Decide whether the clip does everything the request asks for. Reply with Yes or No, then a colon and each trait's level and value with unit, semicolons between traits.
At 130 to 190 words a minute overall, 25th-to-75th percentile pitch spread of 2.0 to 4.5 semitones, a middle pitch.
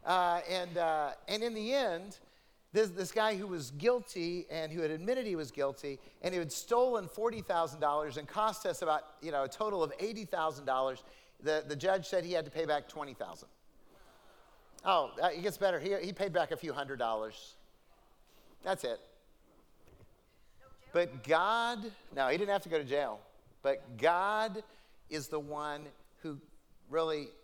No: average, 165 wpm; average, 5.1 semitones; medium, 165 Hz